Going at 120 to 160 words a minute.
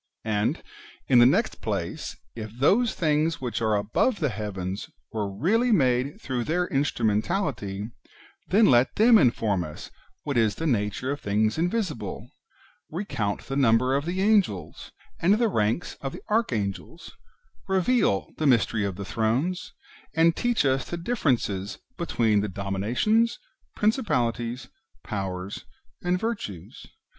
Yes: average, 140 wpm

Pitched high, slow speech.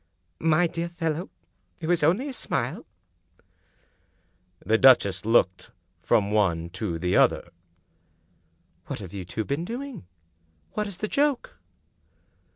No: low, 135 Hz; slow, 125 wpm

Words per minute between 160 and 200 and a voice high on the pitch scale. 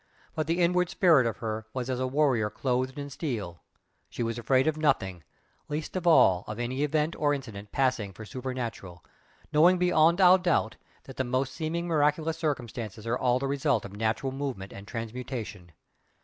No: average, 175 wpm; low, 130 Hz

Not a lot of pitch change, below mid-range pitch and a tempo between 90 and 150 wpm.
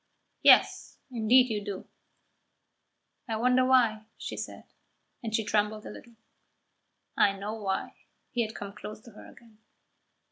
No: narrow, 2.1 semitones; high, 220 Hz; average, 140 wpm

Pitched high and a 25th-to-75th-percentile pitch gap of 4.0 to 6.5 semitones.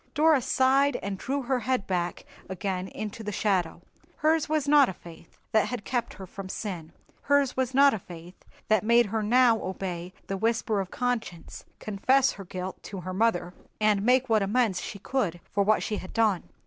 Yes: high, 215 Hz; average, 5.1 semitones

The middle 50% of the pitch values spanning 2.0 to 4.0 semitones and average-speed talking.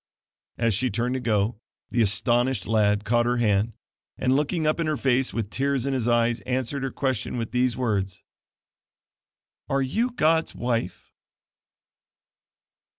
Yes: average, 3.0 semitones; average, 150 wpm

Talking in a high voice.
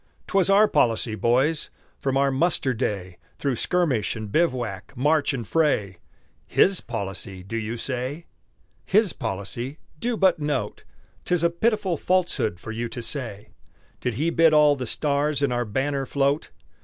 No: low, 135 Hz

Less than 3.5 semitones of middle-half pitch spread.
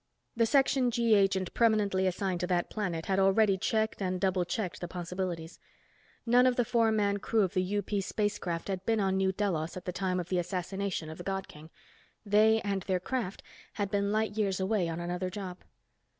Yes: average, 2.8 semitones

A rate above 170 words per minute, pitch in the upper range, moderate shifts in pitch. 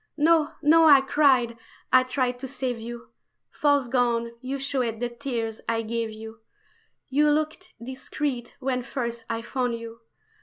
No: average, 150 wpm; very high, 250 Hz; average, 3.0 semitones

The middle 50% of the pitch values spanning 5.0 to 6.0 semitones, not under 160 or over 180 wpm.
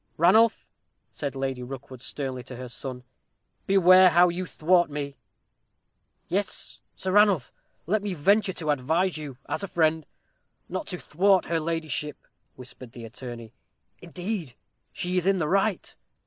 No: wide, 5.6 semitones; average, 145 wpm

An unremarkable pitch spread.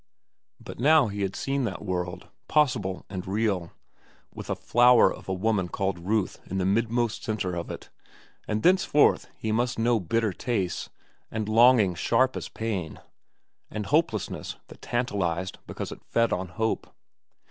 Yes: average, 4.2 semitones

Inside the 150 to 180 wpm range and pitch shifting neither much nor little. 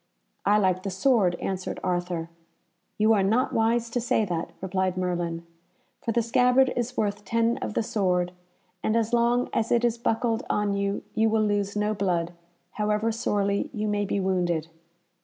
Yes: average, 175 wpm; average, 3.5 semitones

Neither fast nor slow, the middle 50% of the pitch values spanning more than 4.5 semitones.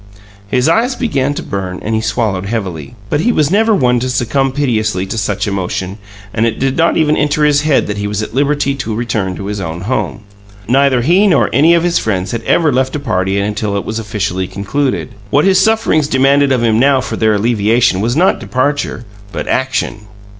No: fast, 210 wpm; wide, 5.6 semitones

